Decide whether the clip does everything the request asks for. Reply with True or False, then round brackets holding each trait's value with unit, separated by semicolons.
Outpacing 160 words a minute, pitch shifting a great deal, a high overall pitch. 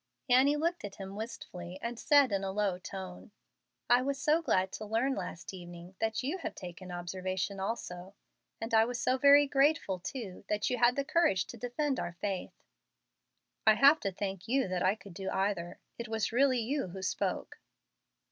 True (190 wpm; 5.8 semitones; 215 Hz)